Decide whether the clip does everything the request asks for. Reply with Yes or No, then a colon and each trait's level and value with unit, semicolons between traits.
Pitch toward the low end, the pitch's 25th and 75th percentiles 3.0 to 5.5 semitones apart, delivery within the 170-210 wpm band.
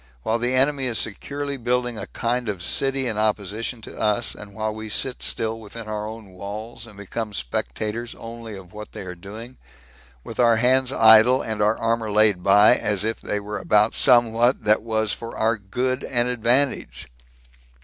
No: low, 110 Hz; narrow, 2.4 semitones; average, 180 wpm